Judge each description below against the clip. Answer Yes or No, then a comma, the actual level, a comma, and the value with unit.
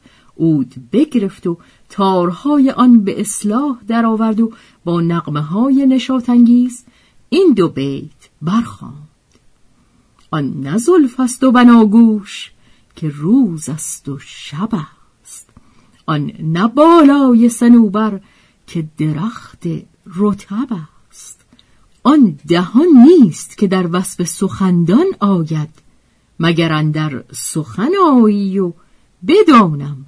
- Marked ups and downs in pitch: Yes, wide, 7.3 semitones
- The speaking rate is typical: No, slow, 95 wpm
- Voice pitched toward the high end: Yes, high, 200 Hz